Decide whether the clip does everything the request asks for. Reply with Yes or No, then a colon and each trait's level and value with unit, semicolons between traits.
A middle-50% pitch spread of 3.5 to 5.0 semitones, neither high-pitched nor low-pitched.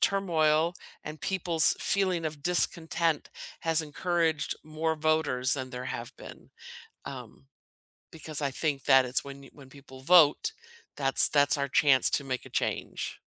No: average, 3.0 semitones; medium, 150 Hz